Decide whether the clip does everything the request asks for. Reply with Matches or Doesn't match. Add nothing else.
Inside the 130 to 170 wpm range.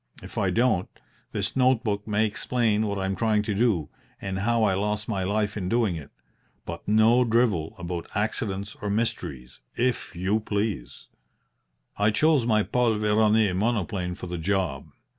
Matches